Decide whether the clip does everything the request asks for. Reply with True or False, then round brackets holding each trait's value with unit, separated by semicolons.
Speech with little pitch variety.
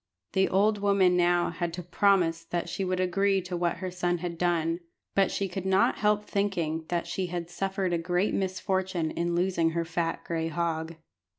True (2.0 semitones)